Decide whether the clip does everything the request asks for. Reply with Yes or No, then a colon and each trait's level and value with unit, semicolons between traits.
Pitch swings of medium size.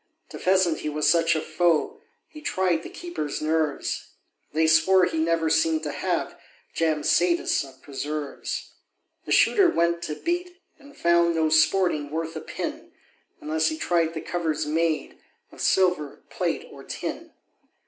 No: narrow, 2.2 semitones